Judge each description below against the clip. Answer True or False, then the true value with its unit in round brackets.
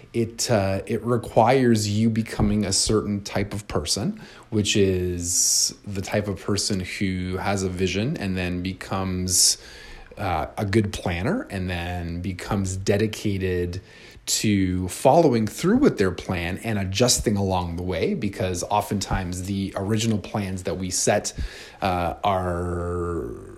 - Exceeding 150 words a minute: False (135 wpm)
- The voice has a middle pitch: False (100 Hz)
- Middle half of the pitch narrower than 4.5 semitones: True (2.9 semitones)